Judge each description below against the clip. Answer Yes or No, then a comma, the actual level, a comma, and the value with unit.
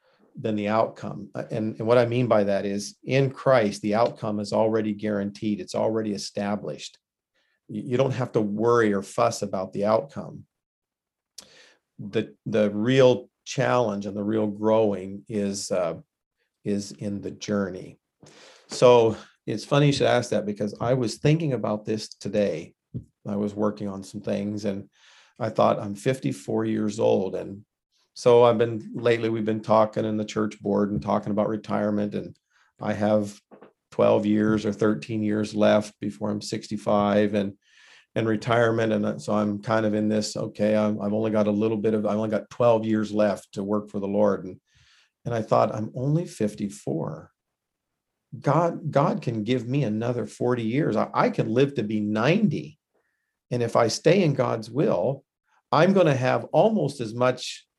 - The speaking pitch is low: Yes, low, 110 Hz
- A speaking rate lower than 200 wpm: Yes, average, 170 wpm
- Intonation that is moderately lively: No, narrow, 2.3 semitones